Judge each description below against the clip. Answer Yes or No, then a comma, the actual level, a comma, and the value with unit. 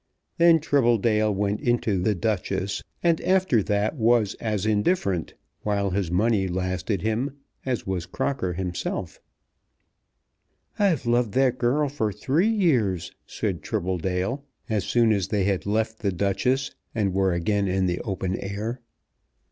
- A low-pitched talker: Yes, low, 105 Hz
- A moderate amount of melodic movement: Yes, average, 4.1 semitones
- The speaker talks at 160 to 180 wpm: No, average, 140 wpm